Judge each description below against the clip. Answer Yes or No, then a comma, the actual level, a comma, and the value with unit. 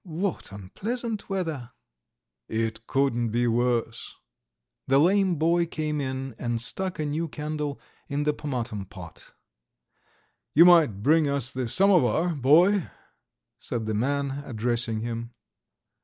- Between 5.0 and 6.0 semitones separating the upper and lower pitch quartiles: Yes, wide, 5.6 semitones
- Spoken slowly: Yes, slow, 125 wpm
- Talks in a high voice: No, medium, 140 Hz